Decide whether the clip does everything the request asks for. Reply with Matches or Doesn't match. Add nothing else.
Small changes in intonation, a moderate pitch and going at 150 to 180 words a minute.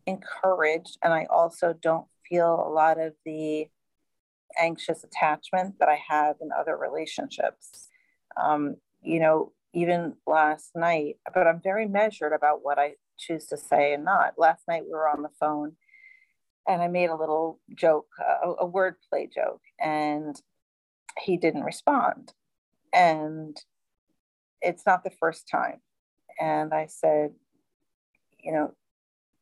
Doesn't match